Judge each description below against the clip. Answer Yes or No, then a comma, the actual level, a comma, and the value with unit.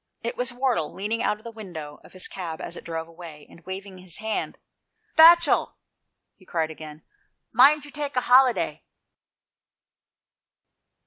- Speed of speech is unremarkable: Yes, average, 150 wpm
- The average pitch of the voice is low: No, high, 200 Hz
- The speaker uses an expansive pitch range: Yes, wide, 7.1 semitones